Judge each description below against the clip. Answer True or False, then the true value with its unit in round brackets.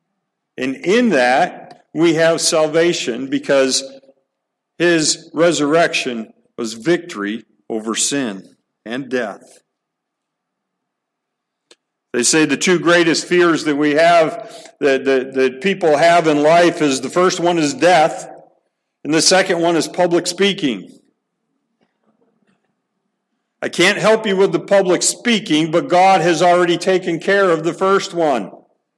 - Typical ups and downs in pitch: True (3.3 semitones)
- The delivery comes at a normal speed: False (130 wpm)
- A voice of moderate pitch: True (170 Hz)